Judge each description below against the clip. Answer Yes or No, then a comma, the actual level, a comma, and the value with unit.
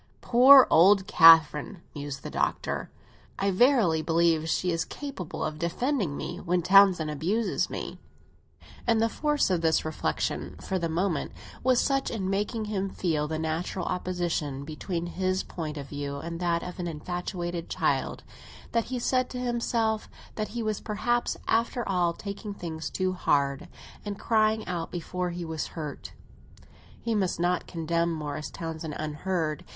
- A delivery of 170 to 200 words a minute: No, average, 155 wpm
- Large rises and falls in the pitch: No, average, 4.7 semitones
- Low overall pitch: No, medium, 180 Hz